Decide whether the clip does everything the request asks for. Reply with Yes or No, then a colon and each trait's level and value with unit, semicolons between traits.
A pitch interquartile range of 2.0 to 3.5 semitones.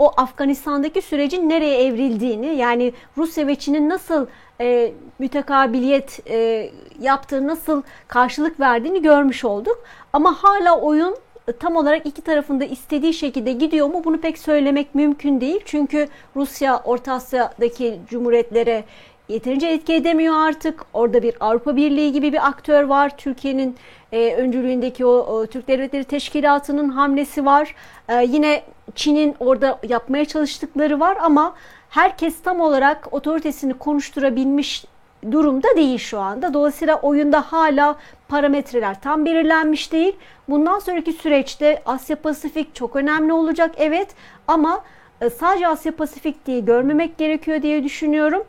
Yes: average, 3.1 semitones